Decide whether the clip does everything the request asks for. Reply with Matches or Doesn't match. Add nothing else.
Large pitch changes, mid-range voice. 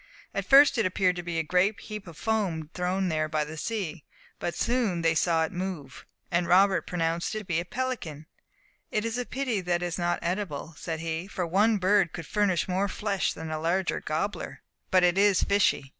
Doesn't match